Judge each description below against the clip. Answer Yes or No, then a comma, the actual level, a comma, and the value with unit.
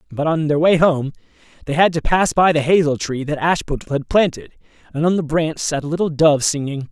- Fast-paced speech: Yes, fast, 225 wpm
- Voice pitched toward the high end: No, medium, 155 Hz